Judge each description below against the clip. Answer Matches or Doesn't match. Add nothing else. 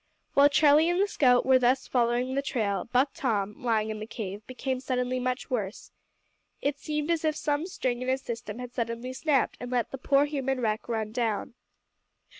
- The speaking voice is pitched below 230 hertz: Doesn't match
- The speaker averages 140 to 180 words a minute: Doesn't match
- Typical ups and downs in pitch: Matches